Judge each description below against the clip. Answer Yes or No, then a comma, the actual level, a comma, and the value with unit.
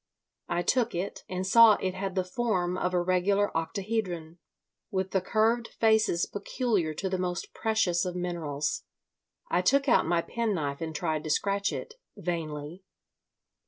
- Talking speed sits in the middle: Yes, average, 150 wpm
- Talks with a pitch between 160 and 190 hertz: Yes, medium, 185 Hz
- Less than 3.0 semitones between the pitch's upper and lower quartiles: No, average, 3.7 semitones